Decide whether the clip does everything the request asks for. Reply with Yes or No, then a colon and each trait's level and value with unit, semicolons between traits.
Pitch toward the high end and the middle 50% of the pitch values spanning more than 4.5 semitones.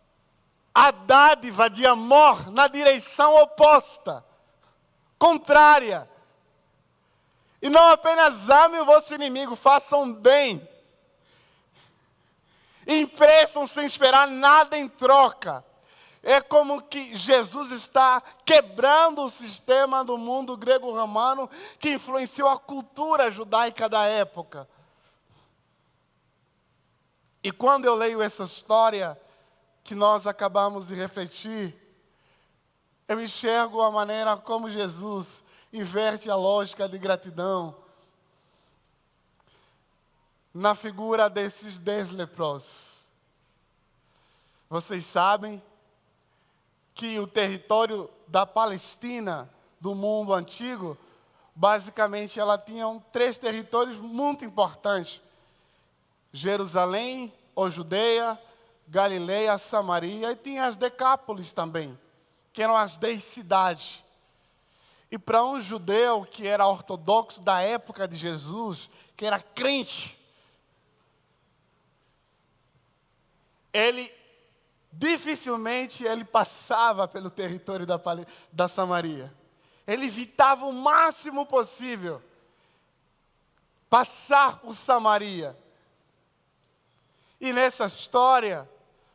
Yes: high, 220 Hz; average, 5.1 semitones